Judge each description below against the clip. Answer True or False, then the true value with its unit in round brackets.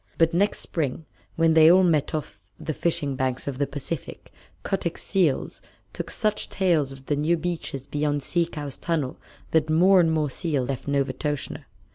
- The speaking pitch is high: False (155 Hz)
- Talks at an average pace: True (170 wpm)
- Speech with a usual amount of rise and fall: True (3.2 semitones)